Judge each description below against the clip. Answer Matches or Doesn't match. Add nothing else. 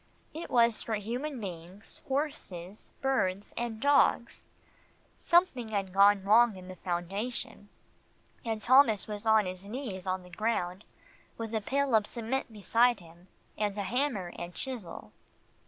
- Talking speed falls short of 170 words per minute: Matches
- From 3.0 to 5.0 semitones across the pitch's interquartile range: Matches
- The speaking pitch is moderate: Doesn't match